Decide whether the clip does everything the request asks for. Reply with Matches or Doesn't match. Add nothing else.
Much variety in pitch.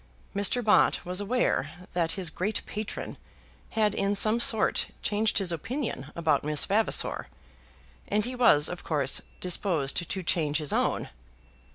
Doesn't match